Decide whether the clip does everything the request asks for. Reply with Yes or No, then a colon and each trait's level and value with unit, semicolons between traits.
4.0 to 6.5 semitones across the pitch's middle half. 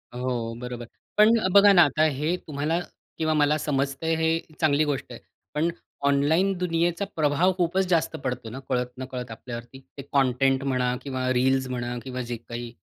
Yes: average, 4.3 semitones